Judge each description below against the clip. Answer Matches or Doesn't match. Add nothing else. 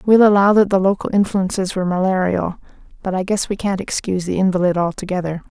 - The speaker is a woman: Matches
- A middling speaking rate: Matches